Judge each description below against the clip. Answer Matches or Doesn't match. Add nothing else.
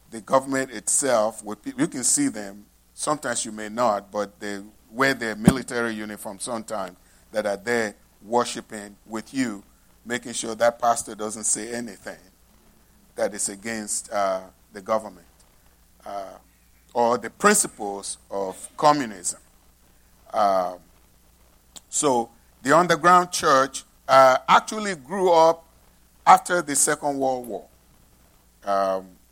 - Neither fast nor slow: Doesn't match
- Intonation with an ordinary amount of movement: Doesn't match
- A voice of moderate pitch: Doesn't match